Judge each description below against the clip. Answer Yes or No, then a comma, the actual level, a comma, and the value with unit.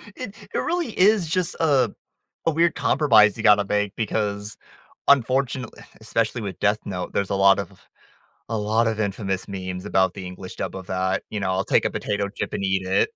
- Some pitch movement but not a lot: Yes, average, 4.0 semitones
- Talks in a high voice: No, low, 105 Hz